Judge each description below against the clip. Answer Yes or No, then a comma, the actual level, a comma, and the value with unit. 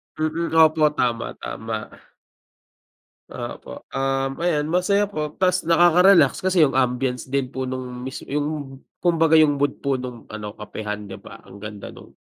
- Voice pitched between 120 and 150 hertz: Yes, medium, 140 Hz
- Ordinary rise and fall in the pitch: Yes, average, 4.5 semitones